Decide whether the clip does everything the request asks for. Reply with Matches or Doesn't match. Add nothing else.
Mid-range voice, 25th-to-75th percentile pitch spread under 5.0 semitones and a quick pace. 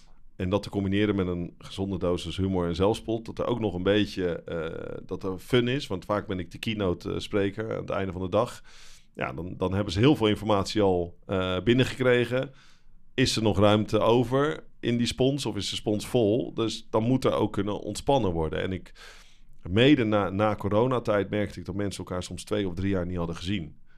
Doesn't match